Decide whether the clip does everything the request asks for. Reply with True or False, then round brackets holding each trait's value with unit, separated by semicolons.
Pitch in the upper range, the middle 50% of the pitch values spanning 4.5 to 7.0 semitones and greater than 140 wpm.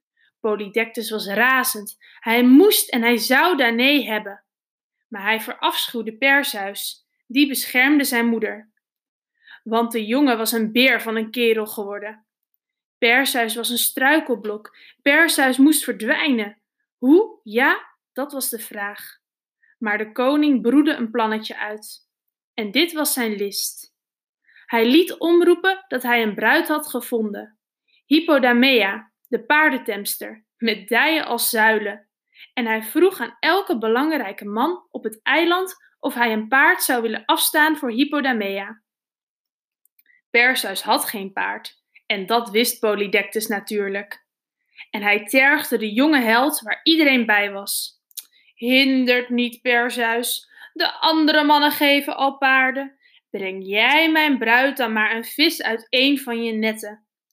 False (240 Hz; 4.8 semitones; 135 wpm)